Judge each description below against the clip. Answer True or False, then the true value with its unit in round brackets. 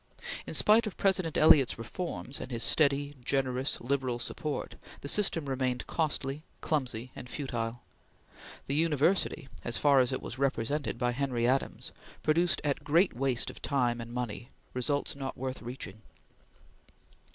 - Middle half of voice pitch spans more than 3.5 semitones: False (3.2 semitones)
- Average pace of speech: True (145 wpm)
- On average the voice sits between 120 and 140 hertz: True (135 Hz)